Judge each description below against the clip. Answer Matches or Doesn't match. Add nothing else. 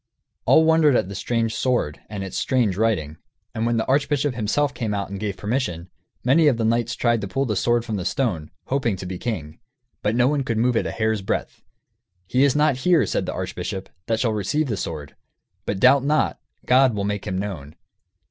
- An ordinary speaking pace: Doesn't match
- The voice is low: Matches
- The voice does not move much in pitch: Doesn't match